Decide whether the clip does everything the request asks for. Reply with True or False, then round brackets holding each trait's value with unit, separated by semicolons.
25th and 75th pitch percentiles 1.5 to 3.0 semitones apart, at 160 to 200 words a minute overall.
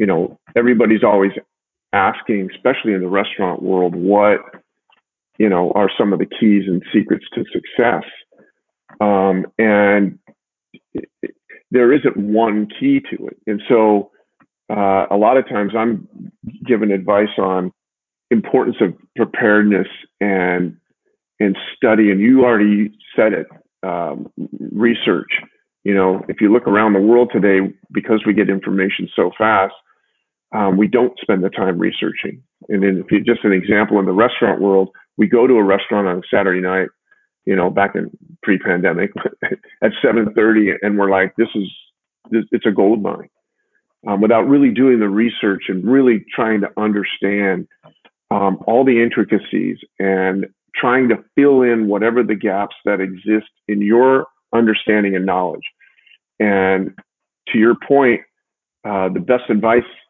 False (2.7 semitones; 150 wpm)